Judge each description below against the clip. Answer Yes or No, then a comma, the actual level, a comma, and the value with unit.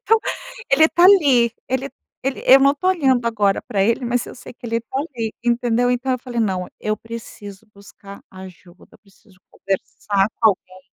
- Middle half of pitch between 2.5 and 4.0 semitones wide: No, average, 4.6 semitones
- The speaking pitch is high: Yes, high, 235 Hz